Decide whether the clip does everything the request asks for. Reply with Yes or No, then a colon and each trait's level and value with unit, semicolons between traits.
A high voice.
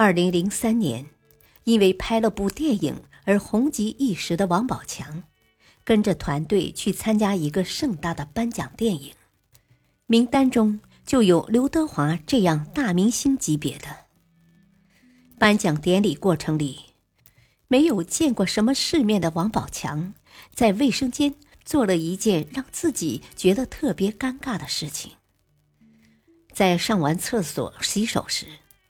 Yes: high, 195 Hz